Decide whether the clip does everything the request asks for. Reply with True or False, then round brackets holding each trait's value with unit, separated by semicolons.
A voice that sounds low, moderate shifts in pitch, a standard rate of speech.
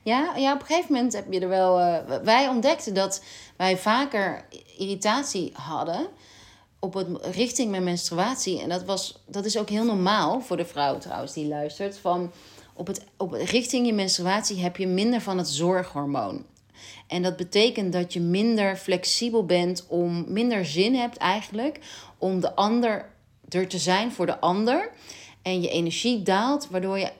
False (190 Hz; 4.0 semitones; 170 wpm)